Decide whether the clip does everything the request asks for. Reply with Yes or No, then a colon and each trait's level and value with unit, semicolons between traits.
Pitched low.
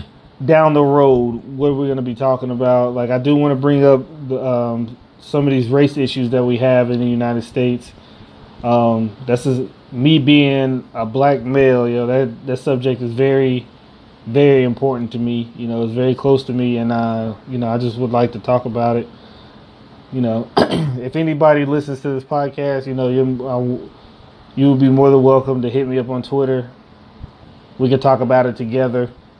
Yes: low, 130 Hz